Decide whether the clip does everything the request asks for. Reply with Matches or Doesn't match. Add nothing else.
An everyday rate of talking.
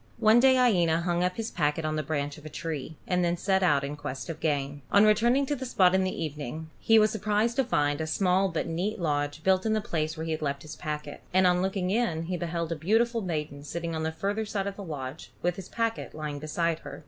Doesn't match